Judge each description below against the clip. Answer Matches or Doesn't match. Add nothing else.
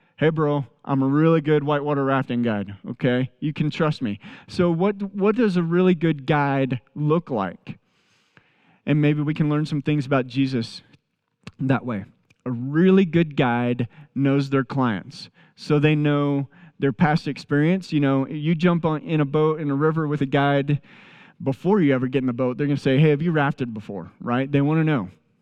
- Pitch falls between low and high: Matches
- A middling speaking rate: Matches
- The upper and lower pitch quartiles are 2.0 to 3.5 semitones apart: Matches